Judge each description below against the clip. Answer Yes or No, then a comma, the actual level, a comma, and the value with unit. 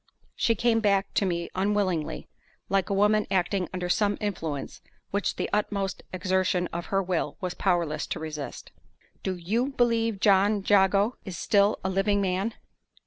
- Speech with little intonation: Yes, narrow, 2.3 semitones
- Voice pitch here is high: Yes, high, 195 Hz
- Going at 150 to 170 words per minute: Yes, average, 155 wpm